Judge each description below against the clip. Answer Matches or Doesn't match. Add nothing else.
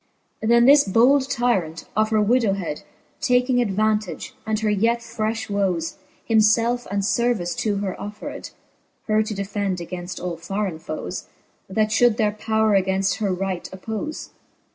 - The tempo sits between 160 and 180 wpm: Doesn't match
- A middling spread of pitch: Matches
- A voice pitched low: Doesn't match